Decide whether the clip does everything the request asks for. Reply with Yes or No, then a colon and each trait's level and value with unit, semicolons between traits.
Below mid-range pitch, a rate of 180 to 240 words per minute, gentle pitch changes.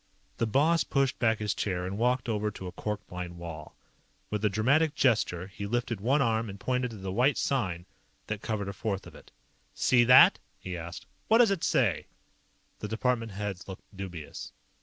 No: low, 105 Hz; average, 190 wpm; average, 4.7 semitones